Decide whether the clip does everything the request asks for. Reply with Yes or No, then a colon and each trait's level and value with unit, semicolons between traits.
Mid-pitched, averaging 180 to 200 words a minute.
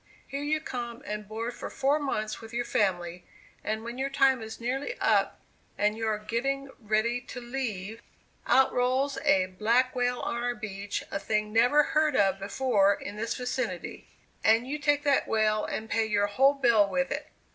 No: high, 235 Hz; average, 185 wpm